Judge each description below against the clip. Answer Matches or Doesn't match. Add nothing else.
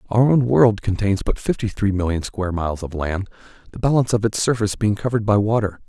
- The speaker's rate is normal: Doesn't match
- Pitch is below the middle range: Matches